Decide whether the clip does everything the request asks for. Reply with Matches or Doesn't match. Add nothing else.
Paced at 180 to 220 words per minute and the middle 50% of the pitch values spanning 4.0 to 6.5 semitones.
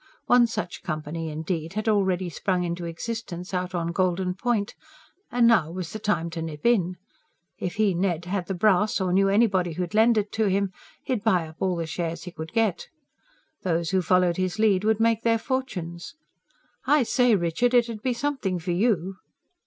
Matches